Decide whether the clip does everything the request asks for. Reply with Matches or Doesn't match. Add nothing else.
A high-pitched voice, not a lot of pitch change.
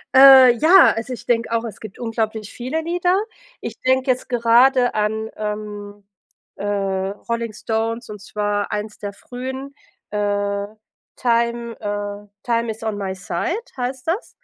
Doesn't match